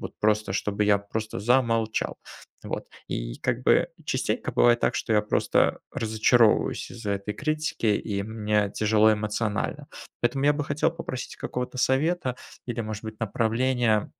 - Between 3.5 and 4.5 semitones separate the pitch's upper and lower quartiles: No, average, 3.0 semitones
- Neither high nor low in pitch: No, low, 110 Hz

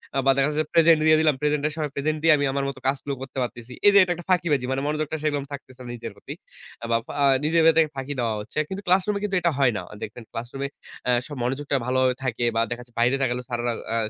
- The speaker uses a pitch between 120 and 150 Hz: Yes, medium, 140 Hz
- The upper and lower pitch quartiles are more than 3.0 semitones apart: Yes, average, 3.9 semitones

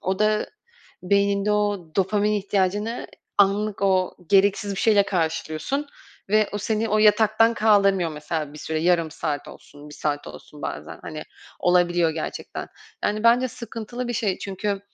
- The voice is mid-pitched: No, high, 200 Hz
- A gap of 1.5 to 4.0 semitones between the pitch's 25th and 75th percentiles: Yes, average, 3.5 semitones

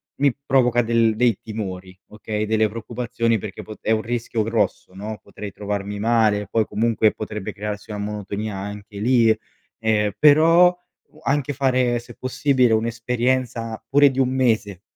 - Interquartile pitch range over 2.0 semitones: Yes, average, 2.8 semitones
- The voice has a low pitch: Yes, low, 110 Hz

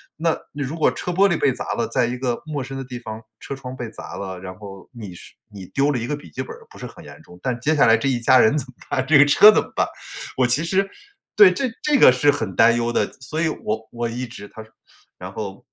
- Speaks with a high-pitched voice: No, low, 130 Hz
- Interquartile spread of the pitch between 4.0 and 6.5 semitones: Yes, average, 4.3 semitones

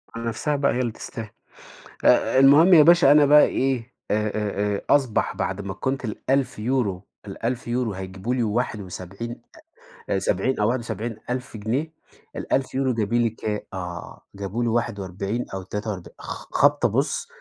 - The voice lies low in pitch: Yes, low, 115 Hz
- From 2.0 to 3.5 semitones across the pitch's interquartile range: No, average, 4.2 semitones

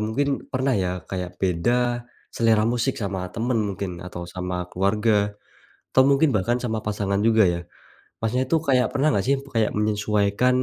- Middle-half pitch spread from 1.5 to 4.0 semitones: No, average, 4.4 semitones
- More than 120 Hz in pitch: No, low, 110 Hz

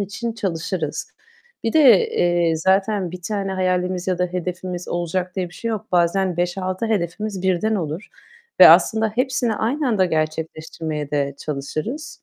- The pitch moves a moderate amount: Yes, average, 3.7 semitones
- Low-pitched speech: No, medium, 185 Hz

